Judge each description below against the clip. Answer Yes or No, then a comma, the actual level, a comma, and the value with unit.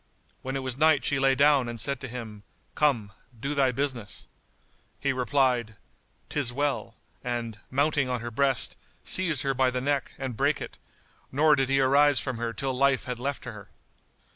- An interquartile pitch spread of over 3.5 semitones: No, narrow, 2.5 semitones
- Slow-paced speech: No, average, 180 wpm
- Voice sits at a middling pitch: No, low, 130 Hz